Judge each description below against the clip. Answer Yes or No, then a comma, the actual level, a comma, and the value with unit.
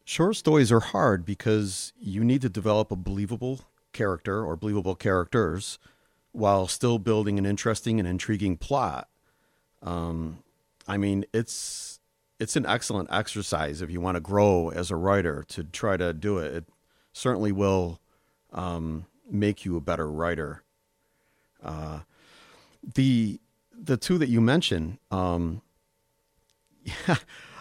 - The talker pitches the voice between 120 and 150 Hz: No, low, 100 Hz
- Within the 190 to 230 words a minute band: No, slow, 135 wpm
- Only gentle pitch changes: No, average, 3.8 semitones